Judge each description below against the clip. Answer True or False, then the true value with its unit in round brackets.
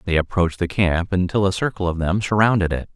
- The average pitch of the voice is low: True (90 Hz)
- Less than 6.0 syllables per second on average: False (6.1 syllables/s)